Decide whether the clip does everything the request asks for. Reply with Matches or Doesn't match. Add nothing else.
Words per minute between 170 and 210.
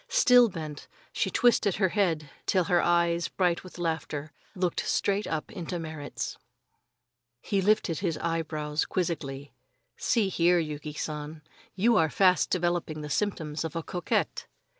Doesn't match